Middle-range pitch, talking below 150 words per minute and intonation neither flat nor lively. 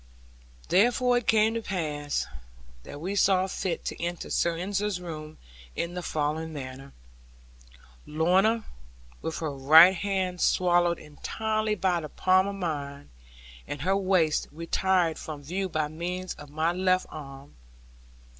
Yes: medium, 175 Hz; slow, 135 wpm; average, 3.7 semitones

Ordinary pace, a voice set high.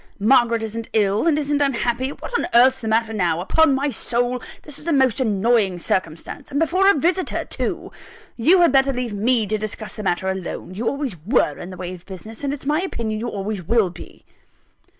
No: fast, 210 wpm; high, 235 Hz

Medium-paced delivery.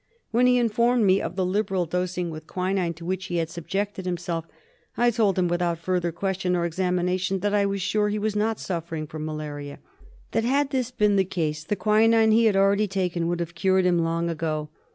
No: fast, 210 wpm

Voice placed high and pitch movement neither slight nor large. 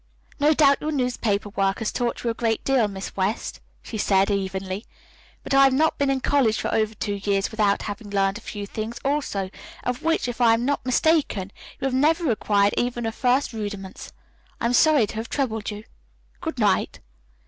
Yes: high, 225 Hz; average, 4.8 semitones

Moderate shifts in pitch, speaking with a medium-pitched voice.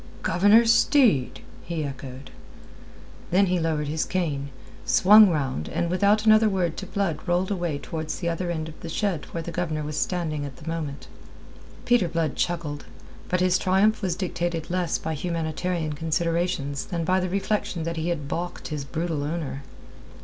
Yes: average, 3.1 semitones; medium, 170 Hz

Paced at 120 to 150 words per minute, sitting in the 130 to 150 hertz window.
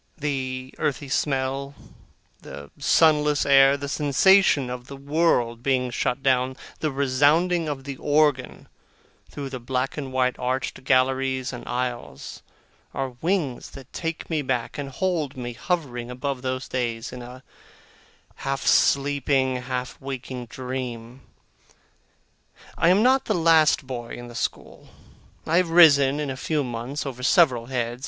Yes: average, 145 wpm; low, 135 Hz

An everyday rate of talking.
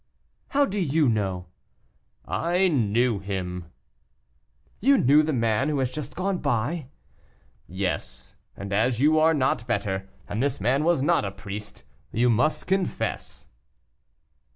No: slow, 130 wpm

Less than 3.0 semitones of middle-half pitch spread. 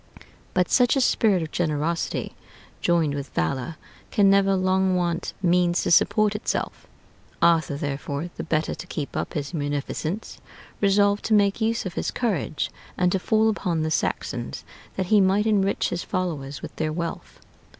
No: average, 4.2 semitones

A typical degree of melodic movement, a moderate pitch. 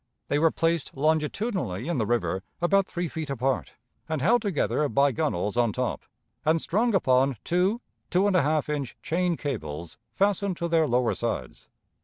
No: wide, 5.7 semitones; medium, 155 Hz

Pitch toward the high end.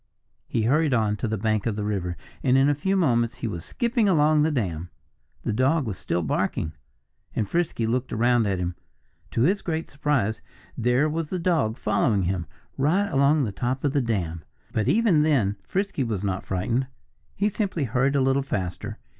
No: low, 125 Hz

